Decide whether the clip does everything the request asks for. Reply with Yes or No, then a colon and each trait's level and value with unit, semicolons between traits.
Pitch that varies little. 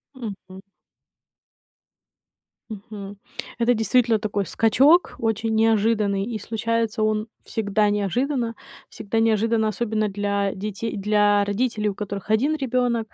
Yes: narrow, 2.0 semitones